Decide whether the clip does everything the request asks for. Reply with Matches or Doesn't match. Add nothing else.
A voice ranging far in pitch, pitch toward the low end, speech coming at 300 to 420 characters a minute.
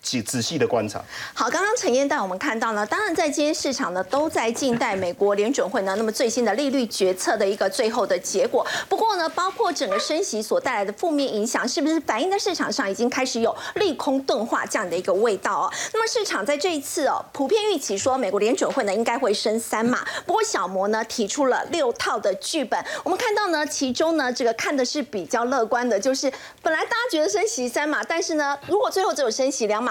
Doesn't match